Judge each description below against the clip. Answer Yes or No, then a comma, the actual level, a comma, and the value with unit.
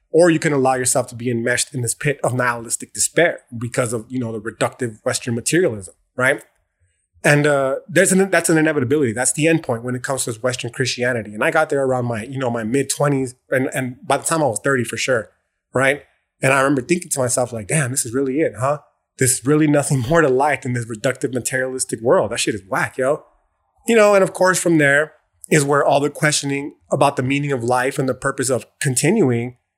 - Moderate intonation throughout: Yes, average, 3.0 semitones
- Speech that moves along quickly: Yes, fast, 225 wpm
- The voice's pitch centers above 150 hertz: No, low, 135 Hz